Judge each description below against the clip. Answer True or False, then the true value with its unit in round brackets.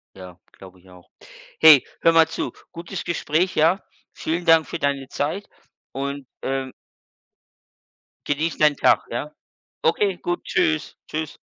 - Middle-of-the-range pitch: True (155 Hz)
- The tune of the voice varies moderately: True (3.6 semitones)